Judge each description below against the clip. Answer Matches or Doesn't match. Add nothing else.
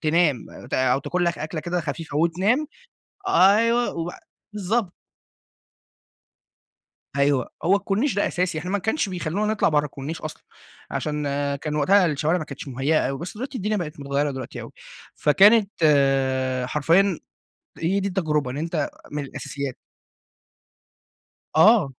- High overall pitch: Doesn't match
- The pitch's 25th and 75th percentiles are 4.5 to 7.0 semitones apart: Matches